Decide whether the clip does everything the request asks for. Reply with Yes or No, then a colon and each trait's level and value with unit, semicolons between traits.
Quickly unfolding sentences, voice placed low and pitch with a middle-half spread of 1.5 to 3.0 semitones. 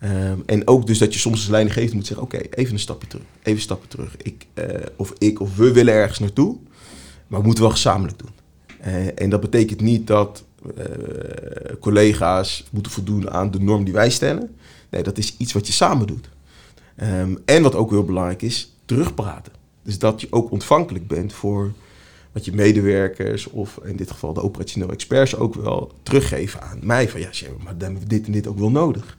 Yes: fast, 210 wpm; low, 105 Hz; narrow, 2.4 semitones